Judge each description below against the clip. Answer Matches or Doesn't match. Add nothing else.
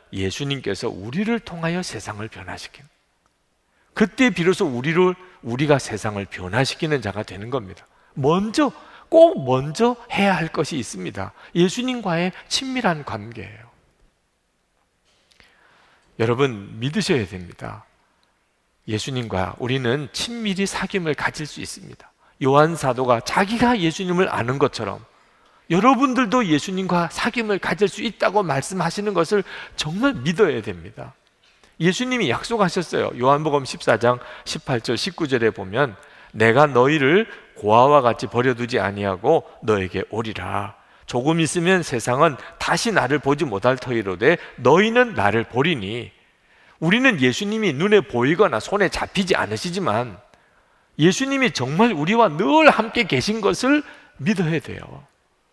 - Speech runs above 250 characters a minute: Matches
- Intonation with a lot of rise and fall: Matches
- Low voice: Doesn't match